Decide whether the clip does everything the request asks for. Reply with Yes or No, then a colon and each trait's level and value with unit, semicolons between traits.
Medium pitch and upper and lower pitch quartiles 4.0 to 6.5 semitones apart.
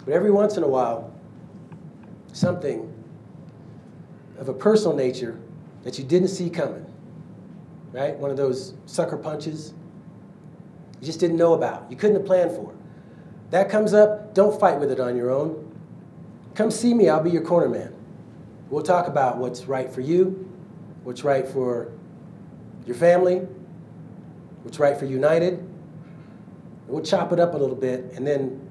Yes: medium, 170 Hz; average, 4.4 semitones